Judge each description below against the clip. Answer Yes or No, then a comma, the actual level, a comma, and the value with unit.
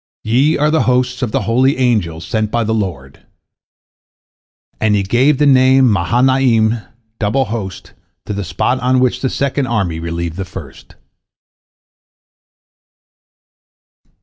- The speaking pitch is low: Yes, low, 115 Hz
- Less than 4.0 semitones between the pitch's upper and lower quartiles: No, average, 4.6 semitones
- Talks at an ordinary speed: No, slow, 130 wpm